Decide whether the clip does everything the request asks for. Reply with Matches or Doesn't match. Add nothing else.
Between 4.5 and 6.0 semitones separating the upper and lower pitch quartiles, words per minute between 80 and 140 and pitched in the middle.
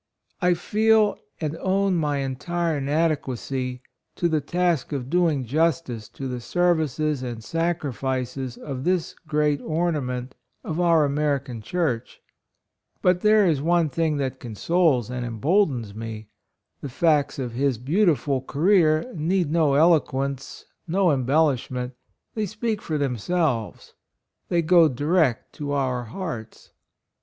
Matches